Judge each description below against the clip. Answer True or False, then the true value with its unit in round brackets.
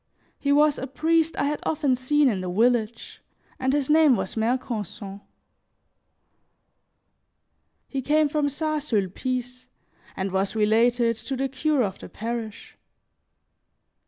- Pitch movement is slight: False (4.8 semitones)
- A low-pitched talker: False (255 Hz)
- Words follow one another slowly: True (130 wpm)